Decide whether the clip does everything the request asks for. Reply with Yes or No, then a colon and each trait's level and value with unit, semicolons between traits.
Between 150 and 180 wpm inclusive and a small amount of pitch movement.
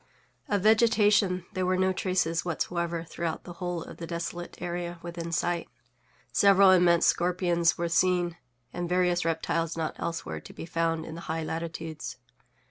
Yes: average, 155 wpm; narrow, 1.6 semitones